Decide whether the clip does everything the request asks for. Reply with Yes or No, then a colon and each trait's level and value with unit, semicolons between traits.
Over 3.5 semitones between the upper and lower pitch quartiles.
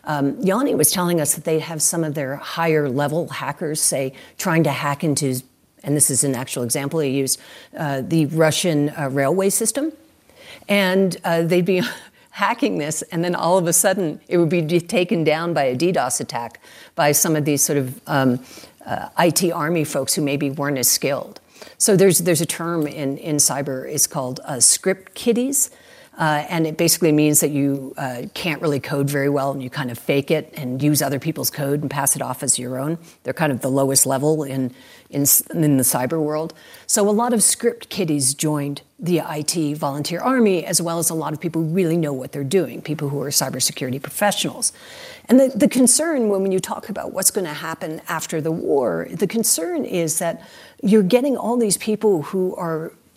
Yes: average, 4.3 semitones